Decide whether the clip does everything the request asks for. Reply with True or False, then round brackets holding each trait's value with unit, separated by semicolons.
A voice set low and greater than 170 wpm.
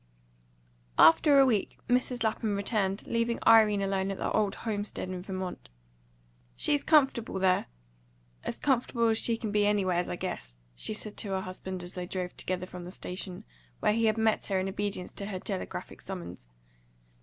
False (200 Hz; 180 wpm)